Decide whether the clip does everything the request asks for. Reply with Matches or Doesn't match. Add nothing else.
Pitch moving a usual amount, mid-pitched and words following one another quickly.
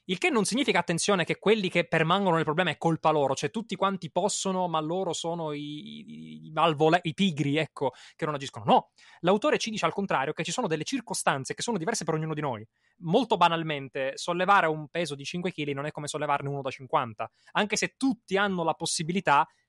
Matches